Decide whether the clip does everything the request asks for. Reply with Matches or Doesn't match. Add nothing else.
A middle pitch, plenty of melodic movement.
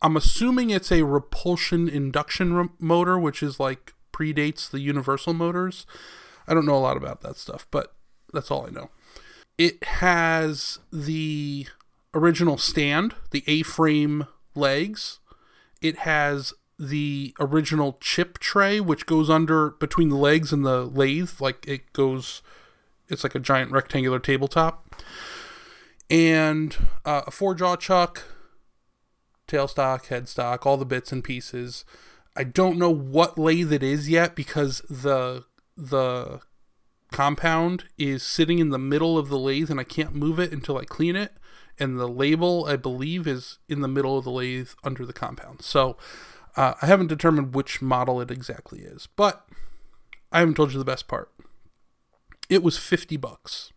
Doesn't match